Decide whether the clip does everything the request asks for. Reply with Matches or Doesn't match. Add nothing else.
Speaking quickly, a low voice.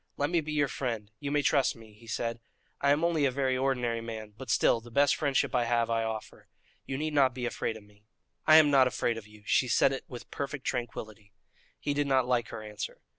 Matches